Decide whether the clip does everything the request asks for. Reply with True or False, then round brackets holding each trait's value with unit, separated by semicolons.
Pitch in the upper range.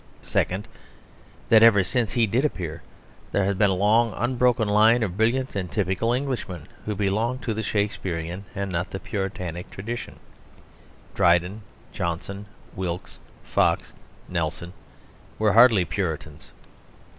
False (100 Hz)